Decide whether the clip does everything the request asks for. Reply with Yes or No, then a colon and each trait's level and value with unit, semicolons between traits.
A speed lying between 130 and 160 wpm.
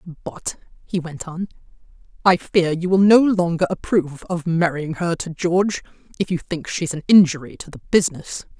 No: average, 175 wpm